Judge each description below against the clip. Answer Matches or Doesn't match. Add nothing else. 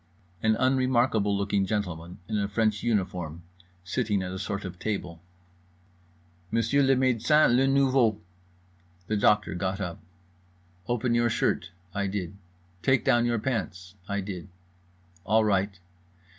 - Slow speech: Matches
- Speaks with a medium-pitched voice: Doesn't match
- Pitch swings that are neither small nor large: Matches